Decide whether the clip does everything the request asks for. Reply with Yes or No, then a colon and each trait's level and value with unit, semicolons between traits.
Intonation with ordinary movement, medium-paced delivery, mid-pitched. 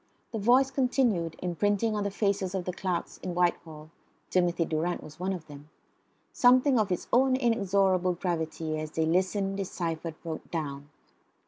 Yes: average, 3.9 semitones; average, 155 wpm; medium, 180 Hz